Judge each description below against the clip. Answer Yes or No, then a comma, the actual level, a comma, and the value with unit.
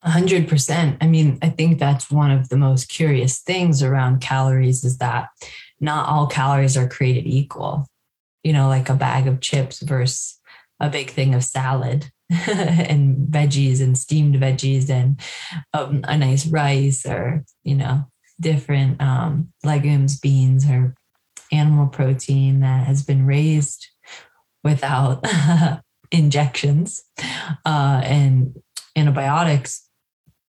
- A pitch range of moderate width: No, narrow, 2.2 semitones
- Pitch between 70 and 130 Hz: No, medium, 140 Hz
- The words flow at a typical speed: No, slow, 125 wpm